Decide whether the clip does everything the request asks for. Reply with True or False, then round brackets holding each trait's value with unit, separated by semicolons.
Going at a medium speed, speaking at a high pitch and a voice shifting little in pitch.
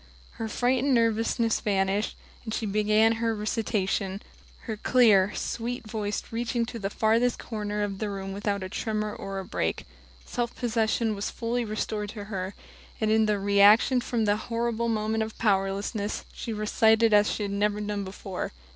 True (170 wpm; 215 Hz; 2.0 semitones)